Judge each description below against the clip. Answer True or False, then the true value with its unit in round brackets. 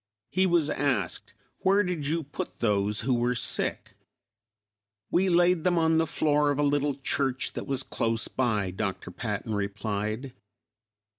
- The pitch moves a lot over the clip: True (6.8 semitones)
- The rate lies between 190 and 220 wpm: False (150 wpm)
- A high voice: False (135 Hz)